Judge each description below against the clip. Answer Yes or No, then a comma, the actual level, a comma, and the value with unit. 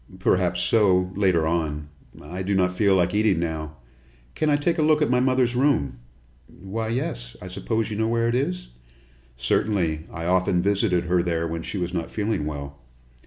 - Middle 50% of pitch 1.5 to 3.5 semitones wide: No, average, 5.1 semitones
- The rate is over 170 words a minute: Yes, average, 185 wpm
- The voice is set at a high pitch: No, very low, 95 Hz